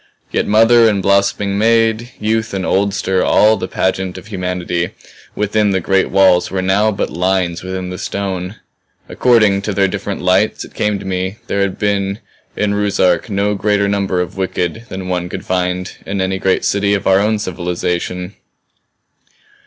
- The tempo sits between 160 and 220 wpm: Yes, average, 170 wpm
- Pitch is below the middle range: Yes, very low, 95 Hz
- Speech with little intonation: Yes, narrow, 1.9 semitones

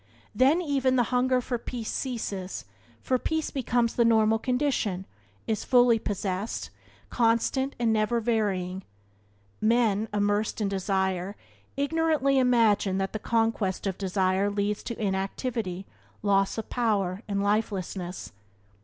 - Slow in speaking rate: Yes, slow, 125 wpm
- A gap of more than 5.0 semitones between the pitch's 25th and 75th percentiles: No, average, 3.9 semitones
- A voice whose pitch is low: No, high, 220 Hz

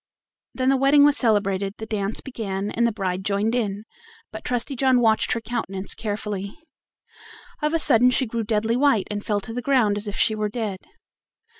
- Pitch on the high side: Yes, high, 220 Hz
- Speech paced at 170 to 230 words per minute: Yes, average, 190 wpm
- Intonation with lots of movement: No, average, 3.3 semitones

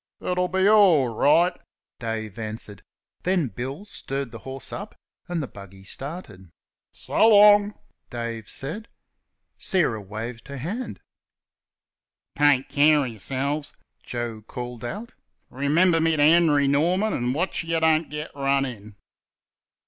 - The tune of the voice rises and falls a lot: Yes, wide, 6.3 semitones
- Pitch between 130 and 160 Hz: Yes, medium, 140 Hz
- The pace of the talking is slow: Yes, slow, 130 wpm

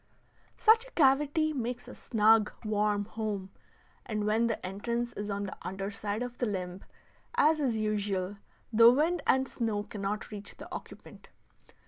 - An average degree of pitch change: Yes, average, 3.3 semitones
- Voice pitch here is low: No, high, 215 Hz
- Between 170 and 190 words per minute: No, average, 155 wpm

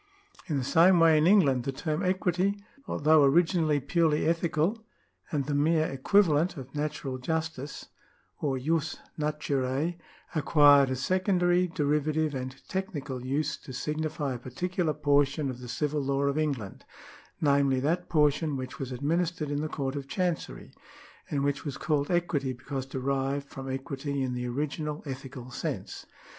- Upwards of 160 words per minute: No, average, 150 wpm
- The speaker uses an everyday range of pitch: Yes, average, 3.0 semitones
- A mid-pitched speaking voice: Yes, medium, 145 Hz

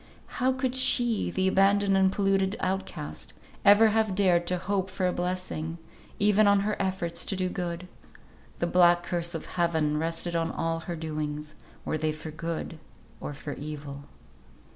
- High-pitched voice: No, medium, 180 Hz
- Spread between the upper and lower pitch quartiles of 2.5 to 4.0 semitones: Yes, average, 3.2 semitones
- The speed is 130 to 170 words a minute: Yes, average, 165 wpm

